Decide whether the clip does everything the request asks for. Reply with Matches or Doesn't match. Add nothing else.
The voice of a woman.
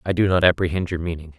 Doesn't match